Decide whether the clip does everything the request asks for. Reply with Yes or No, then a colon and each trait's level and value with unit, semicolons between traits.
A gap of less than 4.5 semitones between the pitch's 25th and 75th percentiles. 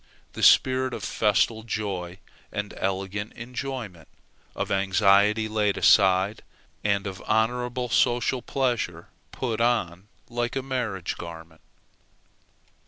Yes: average, 4.0 semitones